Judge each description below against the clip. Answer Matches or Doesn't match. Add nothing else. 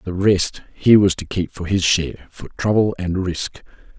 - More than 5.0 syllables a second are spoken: Doesn't match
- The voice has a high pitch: Doesn't match